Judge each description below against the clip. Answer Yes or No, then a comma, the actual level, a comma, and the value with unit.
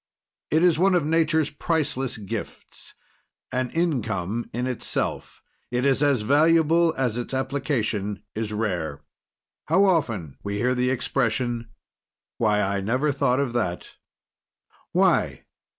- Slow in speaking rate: Yes, slow, 125 wpm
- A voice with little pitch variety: No, wide, 5.6 semitones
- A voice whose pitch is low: Yes, low, 125 Hz